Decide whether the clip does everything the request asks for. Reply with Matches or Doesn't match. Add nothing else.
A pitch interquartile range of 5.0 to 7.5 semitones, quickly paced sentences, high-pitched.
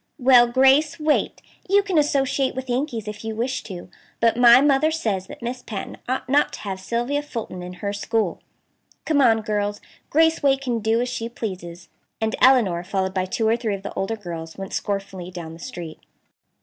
Doesn't match